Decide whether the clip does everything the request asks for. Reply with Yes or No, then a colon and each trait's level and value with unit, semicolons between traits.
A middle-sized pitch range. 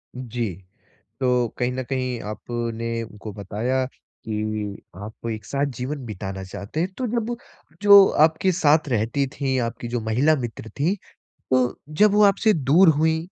No: wide, 5.8 semitones